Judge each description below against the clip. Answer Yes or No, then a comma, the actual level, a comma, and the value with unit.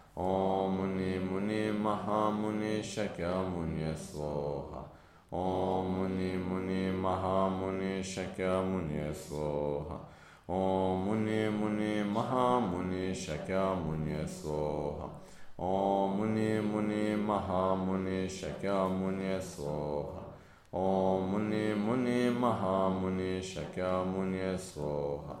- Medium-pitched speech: No, very low, 95 Hz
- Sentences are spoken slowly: Yes, slow, 60 wpm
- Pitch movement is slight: Yes, narrow, 1.8 semitones